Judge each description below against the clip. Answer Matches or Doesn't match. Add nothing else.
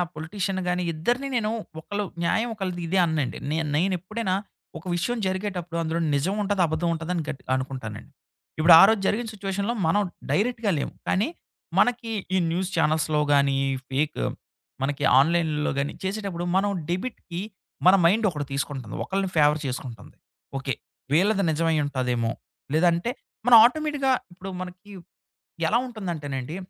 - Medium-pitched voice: Matches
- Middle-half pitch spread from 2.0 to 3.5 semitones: Doesn't match